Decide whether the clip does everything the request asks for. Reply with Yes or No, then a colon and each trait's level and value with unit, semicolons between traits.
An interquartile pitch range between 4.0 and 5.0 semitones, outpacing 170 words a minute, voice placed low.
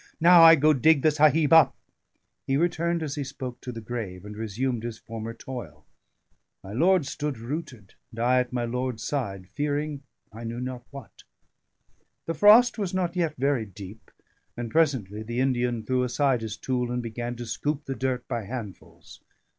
Yes: average, 4.4 semitones; average, 180 wpm; low, 125 Hz